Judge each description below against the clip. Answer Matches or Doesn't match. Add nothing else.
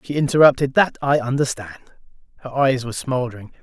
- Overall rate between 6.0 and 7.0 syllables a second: Matches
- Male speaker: Matches